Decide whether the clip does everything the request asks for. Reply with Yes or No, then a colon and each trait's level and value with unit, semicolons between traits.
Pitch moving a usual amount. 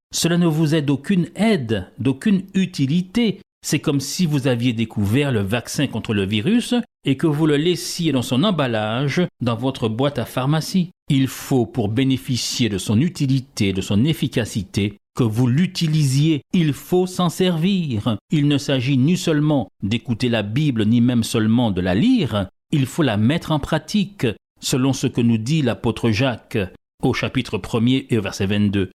No: wide, 5.7 semitones